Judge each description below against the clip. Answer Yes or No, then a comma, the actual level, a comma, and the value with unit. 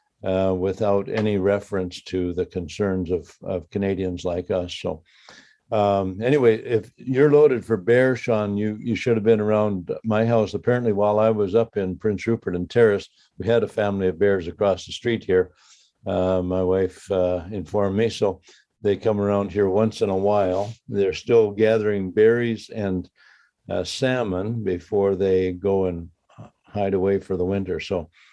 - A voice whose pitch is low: Yes, low, 100 Hz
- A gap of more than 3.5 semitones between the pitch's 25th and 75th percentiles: No, average, 3.0 semitones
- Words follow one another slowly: No, average, 170 wpm